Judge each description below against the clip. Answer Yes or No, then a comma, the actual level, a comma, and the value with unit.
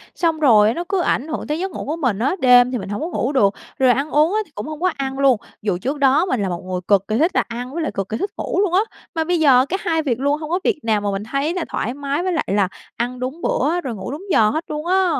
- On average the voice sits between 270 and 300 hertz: Yes, very high, 275 Hz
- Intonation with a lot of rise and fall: Yes, wide, 5.9 semitones